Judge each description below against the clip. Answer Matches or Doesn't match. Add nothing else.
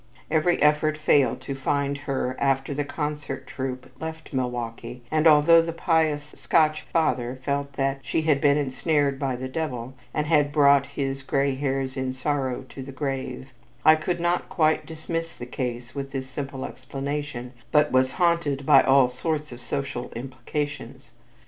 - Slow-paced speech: Doesn't match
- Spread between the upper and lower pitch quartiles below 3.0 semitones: Matches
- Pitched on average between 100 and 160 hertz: Matches